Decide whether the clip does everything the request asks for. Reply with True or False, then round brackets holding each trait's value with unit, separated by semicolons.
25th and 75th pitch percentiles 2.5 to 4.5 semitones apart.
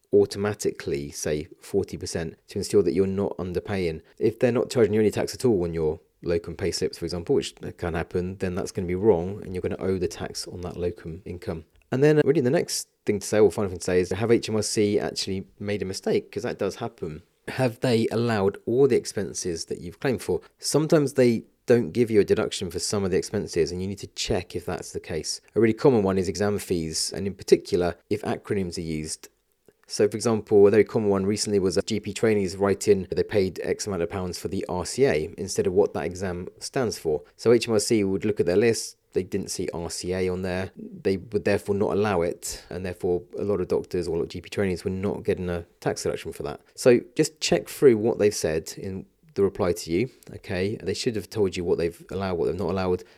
False (5.4 semitones)